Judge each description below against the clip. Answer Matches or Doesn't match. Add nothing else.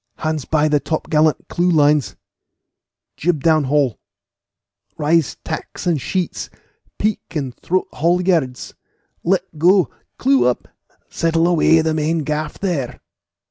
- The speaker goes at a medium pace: Doesn't match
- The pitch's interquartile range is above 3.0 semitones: Doesn't match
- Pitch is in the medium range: Matches